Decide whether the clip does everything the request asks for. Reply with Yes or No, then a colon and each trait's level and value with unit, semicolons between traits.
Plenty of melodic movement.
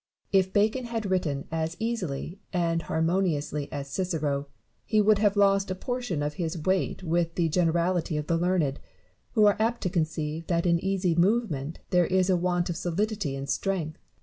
No: average, 3.5 semitones